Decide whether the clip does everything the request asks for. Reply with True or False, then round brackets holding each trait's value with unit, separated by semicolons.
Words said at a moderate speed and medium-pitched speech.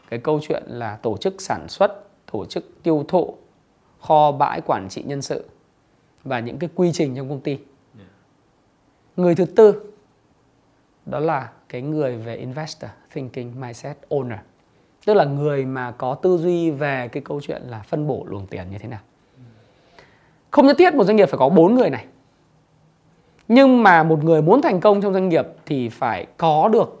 True (180 wpm; 150 Hz)